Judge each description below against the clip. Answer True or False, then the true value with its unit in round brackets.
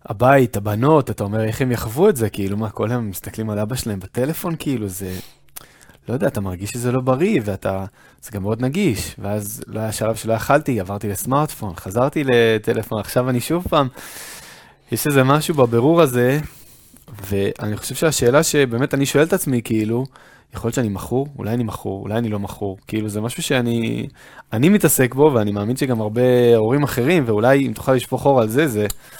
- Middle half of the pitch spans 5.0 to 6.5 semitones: False (4.3 semitones)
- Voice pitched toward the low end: True (120 Hz)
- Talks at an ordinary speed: False (190 wpm)